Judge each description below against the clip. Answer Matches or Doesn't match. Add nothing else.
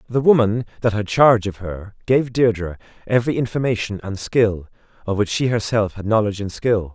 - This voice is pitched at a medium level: Doesn't match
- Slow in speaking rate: Doesn't match